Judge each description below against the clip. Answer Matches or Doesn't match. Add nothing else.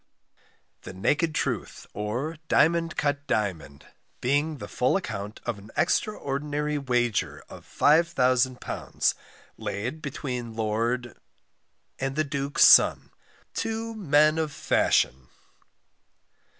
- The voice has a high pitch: Doesn't match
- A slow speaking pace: Matches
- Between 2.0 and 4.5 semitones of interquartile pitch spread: Doesn't match